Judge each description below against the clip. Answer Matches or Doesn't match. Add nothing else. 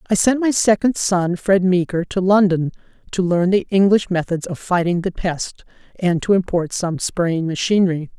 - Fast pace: Doesn't match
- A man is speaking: Doesn't match